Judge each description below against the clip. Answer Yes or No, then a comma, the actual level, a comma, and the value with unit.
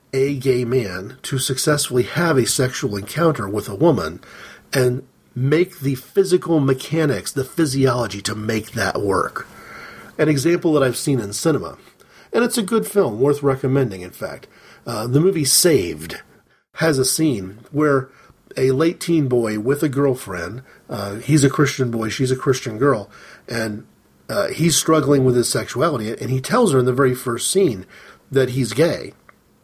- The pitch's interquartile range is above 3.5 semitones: Yes, average, 4.1 semitones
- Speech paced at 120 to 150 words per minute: No, average, 165 wpm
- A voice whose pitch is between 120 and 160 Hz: Yes, low, 135 Hz